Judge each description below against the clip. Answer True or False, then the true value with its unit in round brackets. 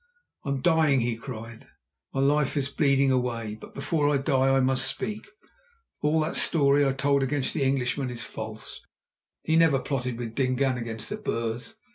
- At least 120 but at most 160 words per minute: False (175 wpm)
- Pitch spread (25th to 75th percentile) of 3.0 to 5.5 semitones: False (2.6 semitones)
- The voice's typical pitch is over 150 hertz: False (135 Hz)